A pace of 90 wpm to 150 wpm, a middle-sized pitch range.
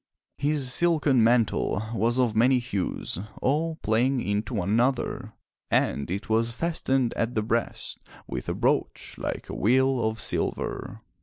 Yes: average, 145 wpm; average, 3.3 semitones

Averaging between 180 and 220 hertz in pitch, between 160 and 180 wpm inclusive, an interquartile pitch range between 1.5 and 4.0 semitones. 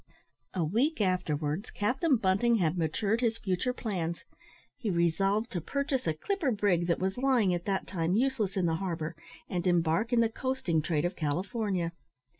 No: high, 190 Hz; average, 170 wpm; average, 5.3 semitones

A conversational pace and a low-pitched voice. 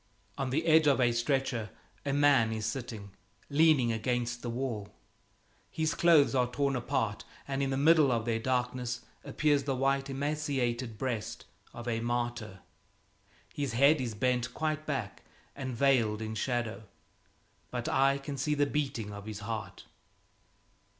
Yes: average, 150 wpm; low, 125 Hz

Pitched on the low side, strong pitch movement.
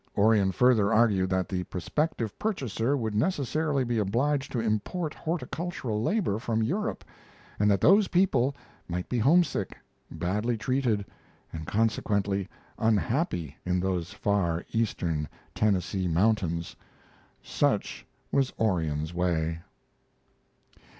Yes: low, 110 Hz; wide, 6.1 semitones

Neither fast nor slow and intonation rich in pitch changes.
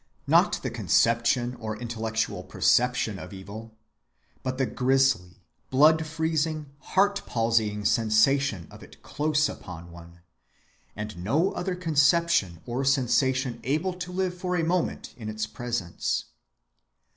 No: slow, 120 wpm; wide, 6.3 semitones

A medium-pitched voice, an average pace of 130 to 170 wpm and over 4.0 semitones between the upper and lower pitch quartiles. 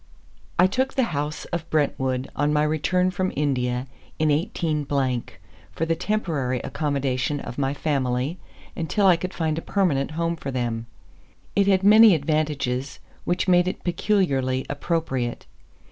Yes: medium, 155 Hz; average, 145 wpm; average, 4.7 semitones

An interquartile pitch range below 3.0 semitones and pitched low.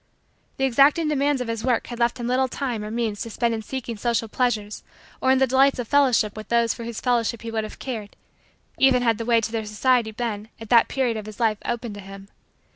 No: narrow, 2.6 semitones; high, 235 Hz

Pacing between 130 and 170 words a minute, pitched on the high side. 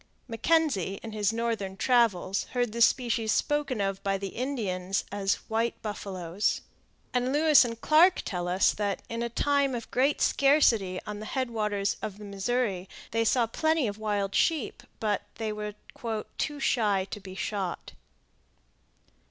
Yes: average, 155 wpm; high, 220 Hz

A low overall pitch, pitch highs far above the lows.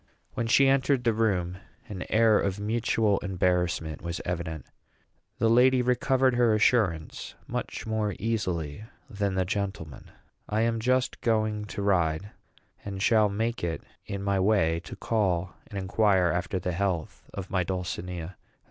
No: low, 100 Hz; average, 3.9 semitones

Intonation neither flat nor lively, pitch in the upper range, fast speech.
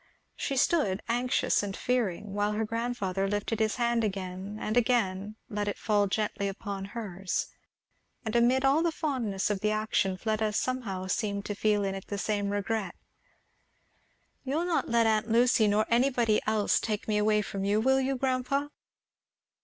No: average, 3.2 semitones; high, 215 Hz; average, 165 wpm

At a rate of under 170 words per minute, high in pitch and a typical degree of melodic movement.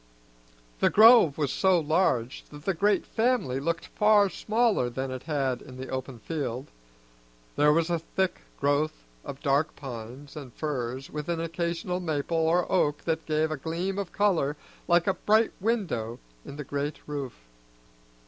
No: average, 160 wpm; medium, 155 Hz; average, 4.7 semitones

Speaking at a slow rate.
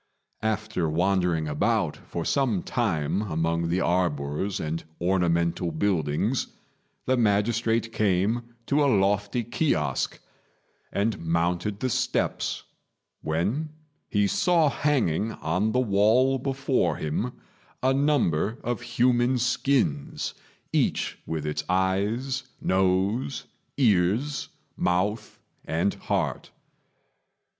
Yes: slow, 100 wpm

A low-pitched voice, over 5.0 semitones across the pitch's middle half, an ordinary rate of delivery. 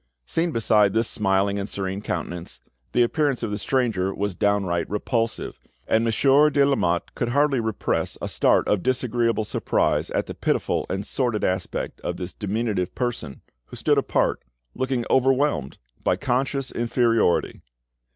No: low, 115 Hz; average, 4.7 semitones; average, 150 wpm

